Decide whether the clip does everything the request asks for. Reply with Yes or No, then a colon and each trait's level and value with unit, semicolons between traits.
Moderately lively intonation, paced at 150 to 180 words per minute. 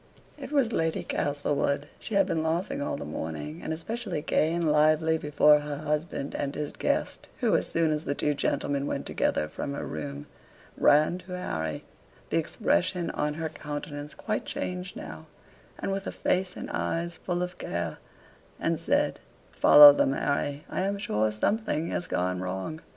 Yes: average, 3.6 semitones; average, 170 wpm